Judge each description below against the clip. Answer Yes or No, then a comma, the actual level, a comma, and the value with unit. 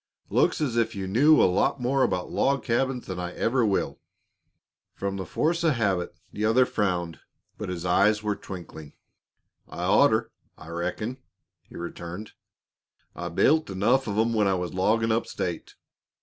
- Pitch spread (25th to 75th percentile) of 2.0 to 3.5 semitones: No, average, 5.0 semitones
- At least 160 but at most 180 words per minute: Yes, average, 165 wpm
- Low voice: Yes, low, 105 Hz